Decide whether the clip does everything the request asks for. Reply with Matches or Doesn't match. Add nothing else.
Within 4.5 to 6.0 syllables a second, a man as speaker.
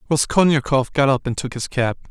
Matches